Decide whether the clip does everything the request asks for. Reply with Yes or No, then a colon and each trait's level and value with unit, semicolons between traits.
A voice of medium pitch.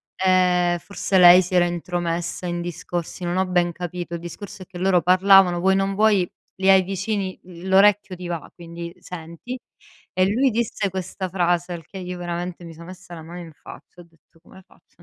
Yes: medium, 180 Hz